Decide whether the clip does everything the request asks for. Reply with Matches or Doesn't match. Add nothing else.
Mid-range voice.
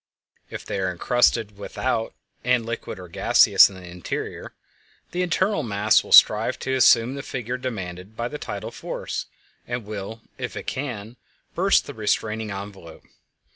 Doesn't match